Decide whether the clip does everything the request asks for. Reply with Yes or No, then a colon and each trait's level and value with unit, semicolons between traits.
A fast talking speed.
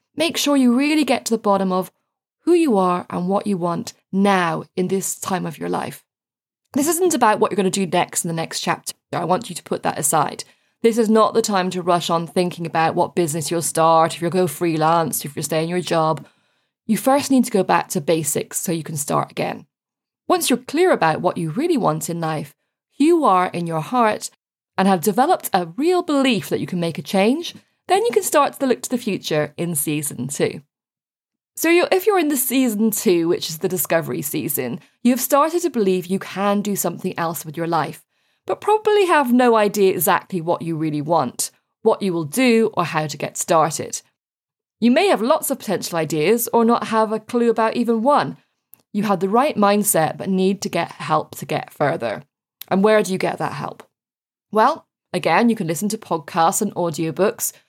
Yes: fast, 215 wpm